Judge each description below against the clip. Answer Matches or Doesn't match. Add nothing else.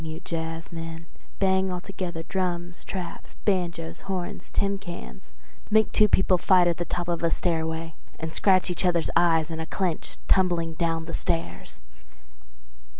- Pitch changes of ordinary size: Doesn't match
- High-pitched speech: Doesn't match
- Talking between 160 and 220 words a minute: Doesn't match